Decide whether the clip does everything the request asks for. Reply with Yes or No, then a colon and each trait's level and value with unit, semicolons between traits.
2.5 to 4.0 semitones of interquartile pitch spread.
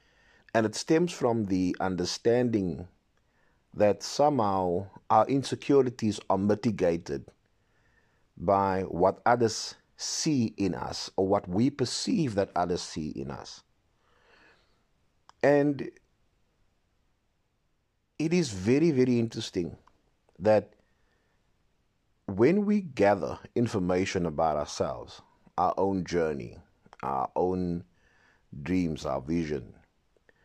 No: average, 4.7 semitones